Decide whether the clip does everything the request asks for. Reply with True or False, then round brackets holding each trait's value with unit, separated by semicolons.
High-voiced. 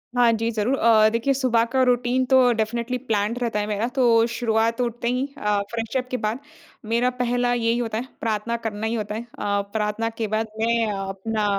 True (230 Hz)